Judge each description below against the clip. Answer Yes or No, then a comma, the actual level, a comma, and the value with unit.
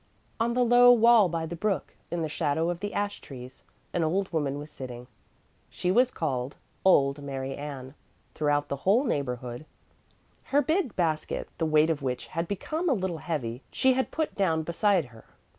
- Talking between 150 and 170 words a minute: No, average, 180 wpm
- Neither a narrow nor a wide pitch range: No, wide, 6.5 semitones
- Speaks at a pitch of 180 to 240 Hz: No, medium, 165 Hz